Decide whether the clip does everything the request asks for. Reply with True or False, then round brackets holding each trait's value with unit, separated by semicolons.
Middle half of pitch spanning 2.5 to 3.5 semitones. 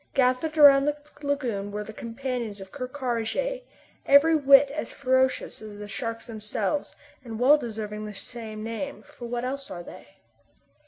False (4.4 semitones)